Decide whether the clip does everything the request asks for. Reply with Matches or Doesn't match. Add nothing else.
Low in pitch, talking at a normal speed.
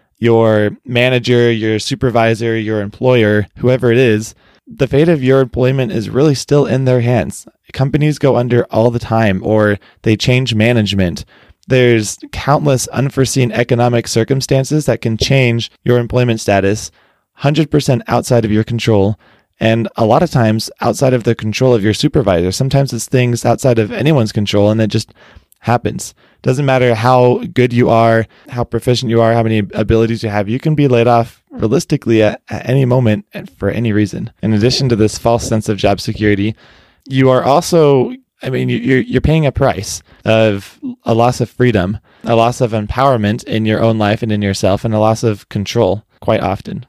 Matches